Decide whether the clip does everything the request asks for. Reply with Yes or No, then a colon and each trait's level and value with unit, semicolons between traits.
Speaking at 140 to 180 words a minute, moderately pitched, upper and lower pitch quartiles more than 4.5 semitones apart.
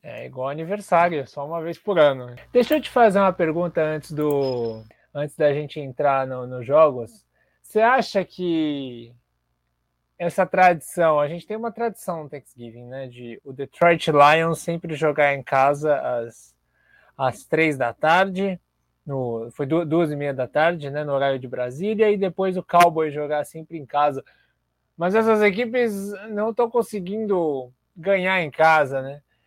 Yes: average, 160 wpm; medium, 155 Hz; wide, 5.6 semitones